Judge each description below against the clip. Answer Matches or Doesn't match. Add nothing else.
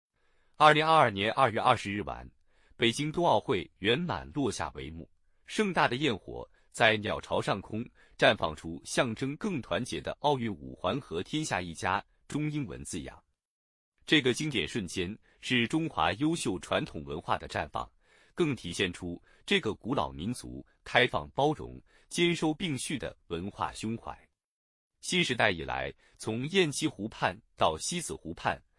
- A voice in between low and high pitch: Doesn't match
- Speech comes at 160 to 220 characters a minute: Doesn't match